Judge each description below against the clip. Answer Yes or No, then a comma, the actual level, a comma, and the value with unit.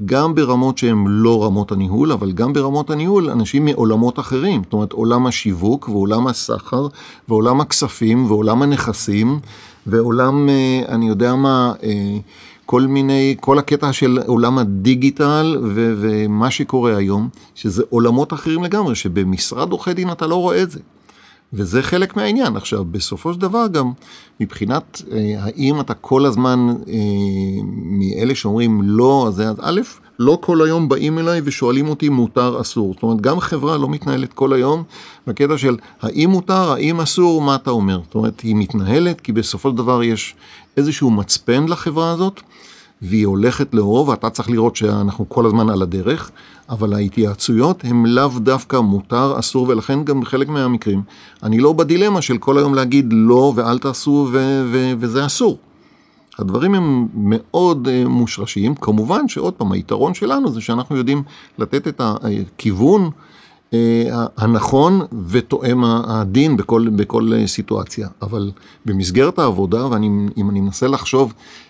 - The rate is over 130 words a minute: Yes, average, 145 wpm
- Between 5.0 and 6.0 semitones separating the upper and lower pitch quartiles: No, average, 4.5 semitones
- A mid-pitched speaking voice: No, low, 125 Hz